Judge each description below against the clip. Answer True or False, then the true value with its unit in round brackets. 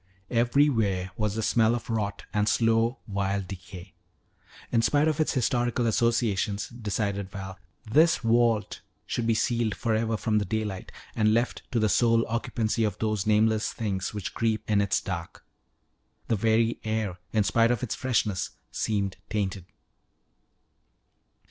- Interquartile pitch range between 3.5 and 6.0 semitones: False (2.5 semitones)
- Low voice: True (110 Hz)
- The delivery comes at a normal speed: True (145 wpm)